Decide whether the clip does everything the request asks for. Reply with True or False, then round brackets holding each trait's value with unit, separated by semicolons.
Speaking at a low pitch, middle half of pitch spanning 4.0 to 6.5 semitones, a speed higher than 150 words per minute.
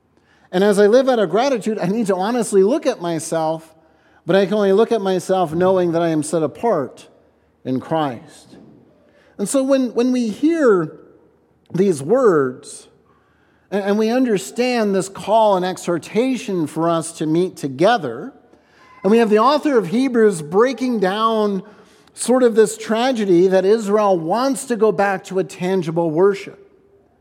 False (200 Hz; 4.5 semitones; 160 wpm)